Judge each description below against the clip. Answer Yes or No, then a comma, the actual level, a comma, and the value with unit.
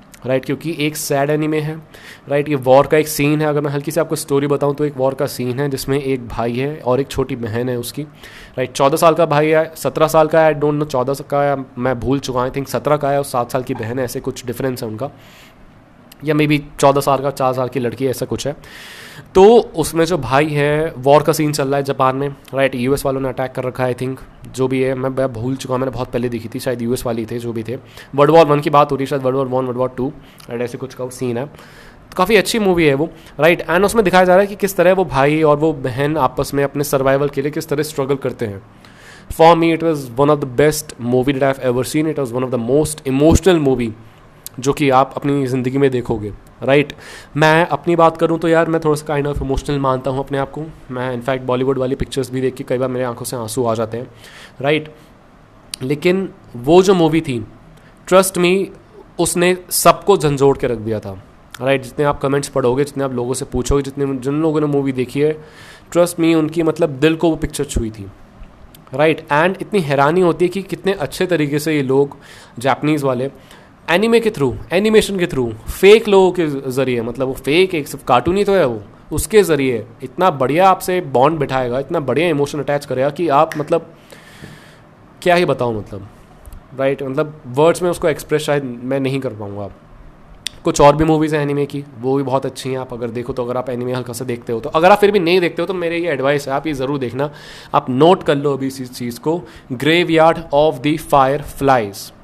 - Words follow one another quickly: Yes, fast, 235 wpm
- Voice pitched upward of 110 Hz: Yes, medium, 140 Hz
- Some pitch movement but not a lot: Yes, average, 3.3 semitones